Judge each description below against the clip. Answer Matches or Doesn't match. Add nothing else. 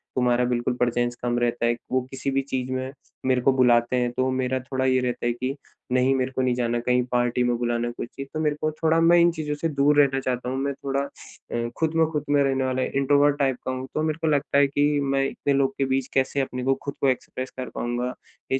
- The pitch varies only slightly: Matches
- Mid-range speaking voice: Doesn't match